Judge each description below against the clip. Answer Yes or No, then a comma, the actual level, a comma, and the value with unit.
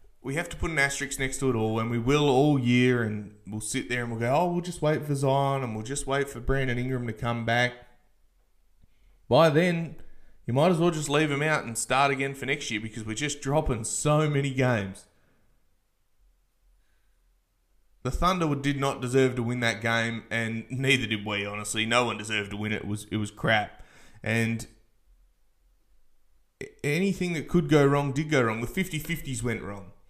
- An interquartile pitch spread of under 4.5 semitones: No, average, 4.8 semitones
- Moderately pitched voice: No, low, 125 Hz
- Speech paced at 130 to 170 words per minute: No, average, 200 wpm